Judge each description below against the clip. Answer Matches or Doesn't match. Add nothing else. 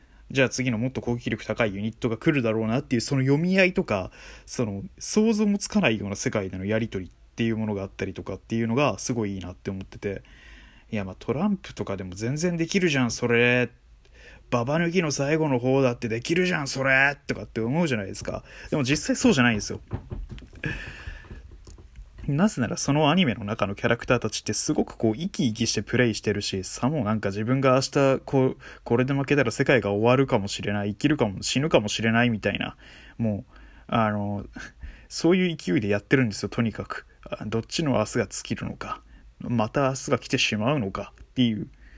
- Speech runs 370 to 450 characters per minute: Matches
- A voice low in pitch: Matches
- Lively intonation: Doesn't match